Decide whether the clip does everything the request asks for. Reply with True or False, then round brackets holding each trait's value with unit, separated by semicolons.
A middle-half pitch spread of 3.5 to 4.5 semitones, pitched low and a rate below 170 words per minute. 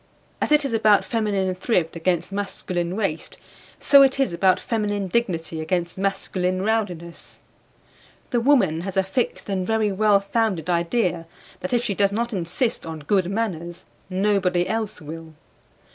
False (4.0 semitones; 195 Hz; 150 wpm)